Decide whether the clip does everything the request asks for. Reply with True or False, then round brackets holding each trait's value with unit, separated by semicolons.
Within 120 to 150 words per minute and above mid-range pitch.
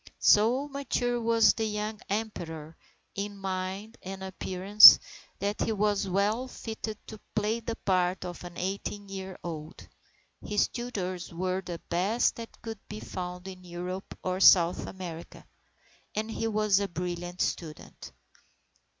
True (140 wpm; 195 Hz)